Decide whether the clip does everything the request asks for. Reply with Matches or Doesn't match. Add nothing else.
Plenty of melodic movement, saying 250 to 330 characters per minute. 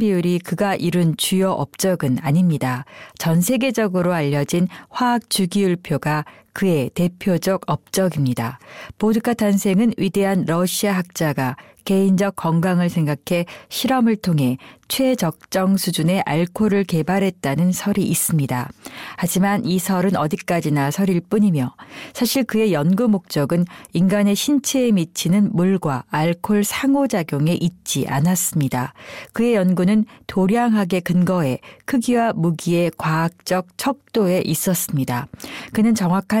Doesn't match